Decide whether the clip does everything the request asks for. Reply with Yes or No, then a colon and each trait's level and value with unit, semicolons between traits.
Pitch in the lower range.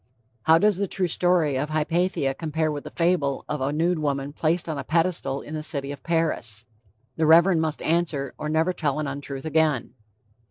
No: medium, 155 Hz